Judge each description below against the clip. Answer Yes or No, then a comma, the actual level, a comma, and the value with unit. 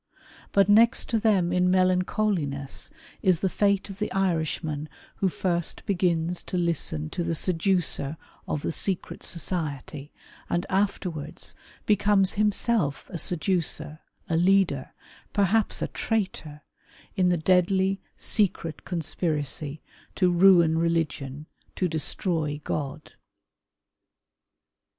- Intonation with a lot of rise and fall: No, average, 3.7 semitones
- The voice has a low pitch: No, medium, 175 Hz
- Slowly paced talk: Yes, slow, 110 wpm